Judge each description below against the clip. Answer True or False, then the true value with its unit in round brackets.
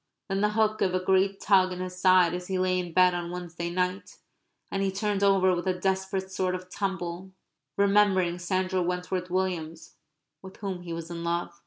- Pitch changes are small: True (1.3 semitones)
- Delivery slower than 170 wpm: False (195 wpm)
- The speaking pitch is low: False (185 Hz)